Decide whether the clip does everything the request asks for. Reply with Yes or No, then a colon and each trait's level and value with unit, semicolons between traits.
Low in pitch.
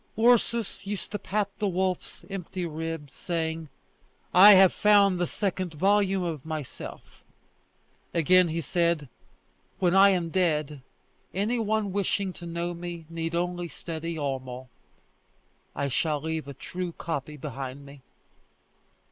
No: medium, 170 Hz